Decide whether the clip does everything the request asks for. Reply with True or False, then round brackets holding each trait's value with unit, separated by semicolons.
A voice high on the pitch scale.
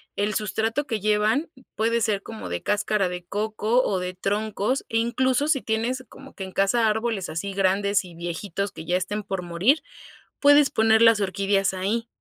True (210 Hz)